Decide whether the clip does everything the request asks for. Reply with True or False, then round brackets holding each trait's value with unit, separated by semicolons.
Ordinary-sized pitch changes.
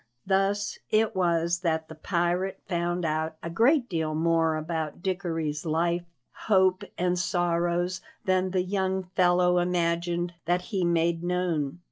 False (1.8 semitones)